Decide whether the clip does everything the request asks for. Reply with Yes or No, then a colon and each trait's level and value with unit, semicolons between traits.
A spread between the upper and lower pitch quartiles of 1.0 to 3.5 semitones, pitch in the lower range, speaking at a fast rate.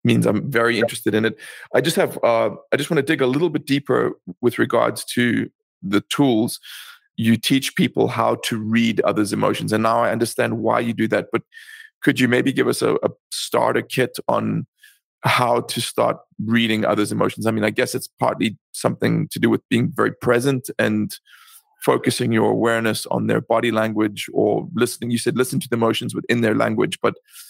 No: narrow, 2.4 semitones; low, 115 Hz; average, 195 wpm